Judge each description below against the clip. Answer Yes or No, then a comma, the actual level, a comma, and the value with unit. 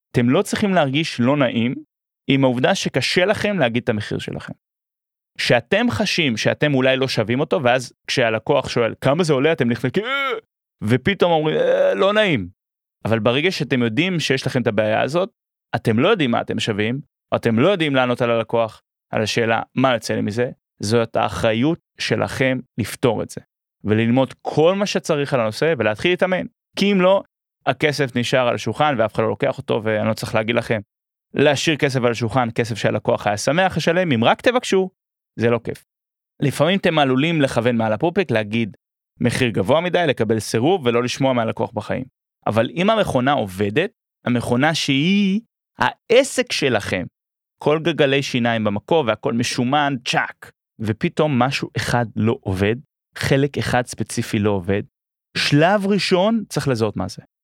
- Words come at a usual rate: No, fast, 165 wpm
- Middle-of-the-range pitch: No, low, 130 Hz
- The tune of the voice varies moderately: No, wide, 6.1 semitones